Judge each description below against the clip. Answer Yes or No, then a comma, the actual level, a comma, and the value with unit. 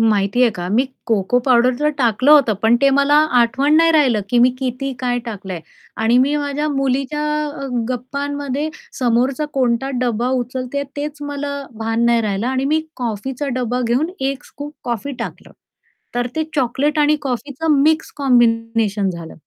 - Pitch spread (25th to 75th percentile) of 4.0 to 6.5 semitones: No, average, 3.4 semitones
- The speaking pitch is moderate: No, very high, 255 Hz